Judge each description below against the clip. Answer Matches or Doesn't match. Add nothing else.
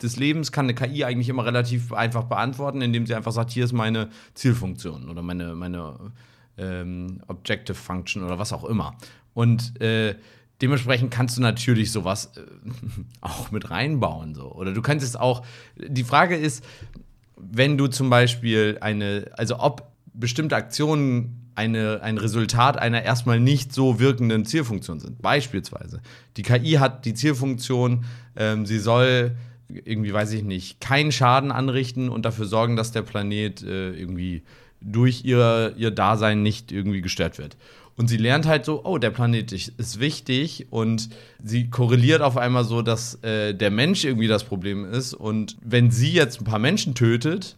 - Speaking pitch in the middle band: Doesn't match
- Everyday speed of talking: Matches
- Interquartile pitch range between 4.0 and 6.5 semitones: Doesn't match